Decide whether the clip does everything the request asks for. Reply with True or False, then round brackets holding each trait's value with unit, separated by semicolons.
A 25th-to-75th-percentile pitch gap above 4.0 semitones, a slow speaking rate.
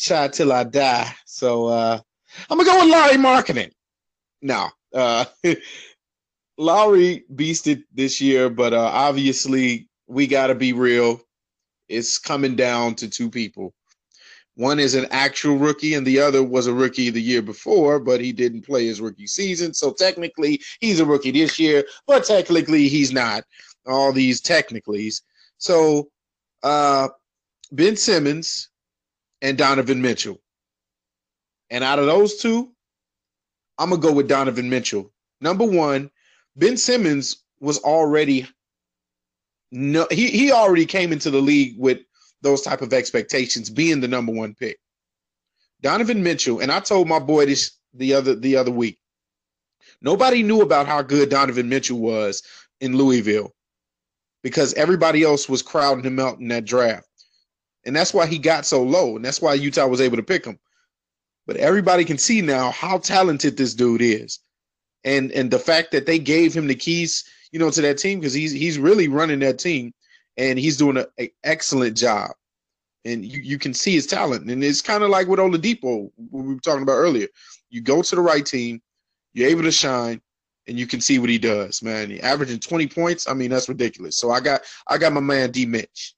False (4.6 semitones; 175 wpm)